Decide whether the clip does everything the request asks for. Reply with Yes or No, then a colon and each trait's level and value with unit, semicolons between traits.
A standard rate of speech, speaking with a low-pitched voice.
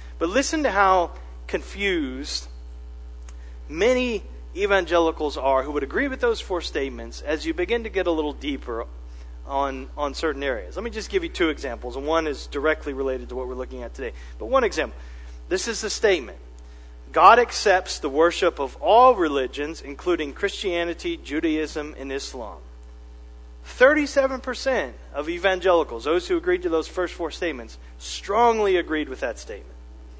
No: average, 160 wpm; medium, 150 Hz